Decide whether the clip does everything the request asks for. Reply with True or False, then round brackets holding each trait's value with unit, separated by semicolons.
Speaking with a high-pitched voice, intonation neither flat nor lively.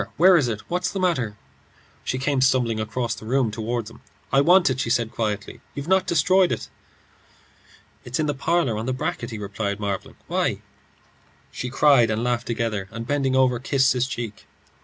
False (125 Hz; 4.0 semitones)